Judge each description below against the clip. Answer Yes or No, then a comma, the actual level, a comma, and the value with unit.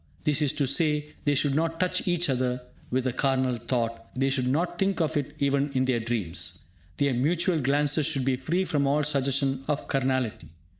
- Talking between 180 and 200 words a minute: Yes, average, 195 wpm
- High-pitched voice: No, medium, 140 Hz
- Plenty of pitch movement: No, average, 2.7 semitones